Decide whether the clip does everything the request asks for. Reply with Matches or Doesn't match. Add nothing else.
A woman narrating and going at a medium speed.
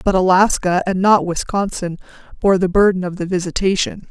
Matches